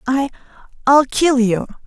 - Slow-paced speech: Yes, slow, 130 wpm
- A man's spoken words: No, female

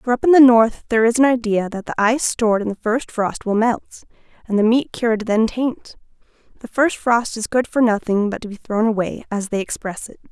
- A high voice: Yes, high, 225 Hz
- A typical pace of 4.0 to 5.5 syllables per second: No, 5.7 syllables/s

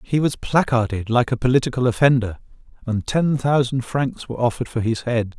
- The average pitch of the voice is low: Yes, low, 125 Hz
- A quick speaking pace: No, average, 180 wpm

